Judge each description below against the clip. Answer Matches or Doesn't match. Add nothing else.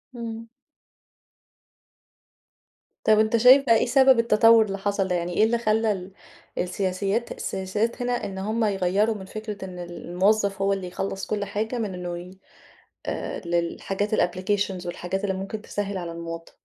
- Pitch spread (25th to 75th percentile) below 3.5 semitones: Matches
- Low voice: Doesn't match